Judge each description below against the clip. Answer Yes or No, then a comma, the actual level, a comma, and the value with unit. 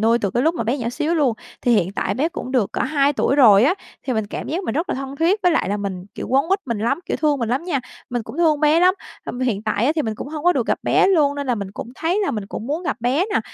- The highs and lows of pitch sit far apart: Yes, wide, 5.7 semitones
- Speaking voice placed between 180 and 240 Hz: No, very high, 270 Hz